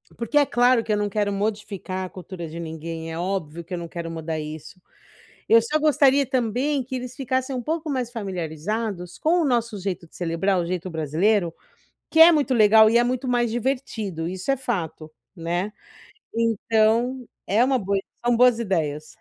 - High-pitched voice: Yes, high, 215 Hz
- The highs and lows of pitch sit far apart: Yes, wide, 6.2 semitones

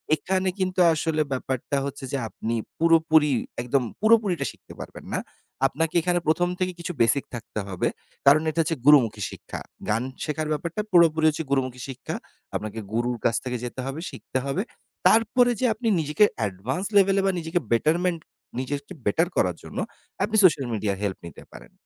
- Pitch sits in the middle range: Yes, medium, 155 Hz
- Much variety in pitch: Yes, wide, 5.8 semitones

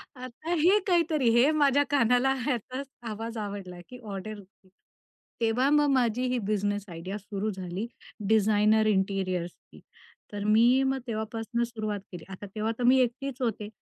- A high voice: Yes, high, 225 Hz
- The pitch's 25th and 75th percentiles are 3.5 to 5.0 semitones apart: Yes, average, 3.8 semitones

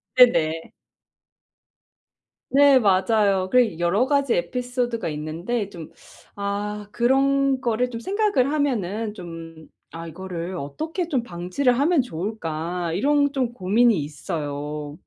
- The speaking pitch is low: No, high, 210 Hz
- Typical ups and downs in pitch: No, wide, 6.9 semitones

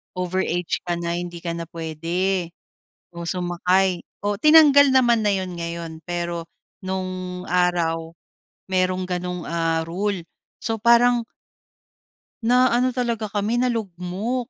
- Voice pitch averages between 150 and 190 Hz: Yes, medium, 185 Hz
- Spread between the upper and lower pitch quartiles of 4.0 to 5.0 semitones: Yes, average, 4.7 semitones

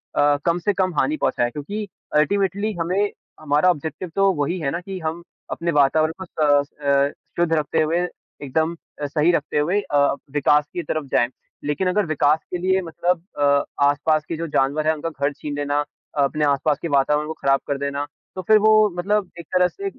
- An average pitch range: Yes, average, 3.8 semitones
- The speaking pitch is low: No, medium, 155 Hz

